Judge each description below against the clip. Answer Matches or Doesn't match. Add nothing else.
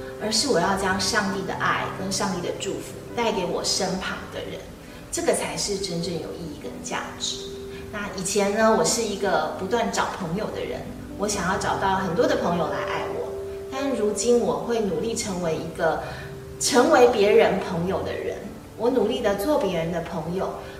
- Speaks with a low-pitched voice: Doesn't match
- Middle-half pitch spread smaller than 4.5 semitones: Doesn't match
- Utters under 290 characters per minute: Matches